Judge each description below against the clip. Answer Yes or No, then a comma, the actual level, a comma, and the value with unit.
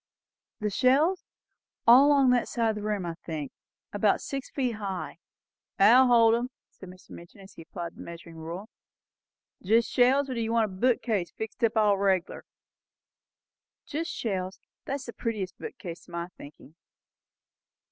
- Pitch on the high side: Yes, high, 215 Hz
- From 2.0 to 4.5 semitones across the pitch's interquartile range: No, average, 5.1 semitones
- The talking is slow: No, average, 165 wpm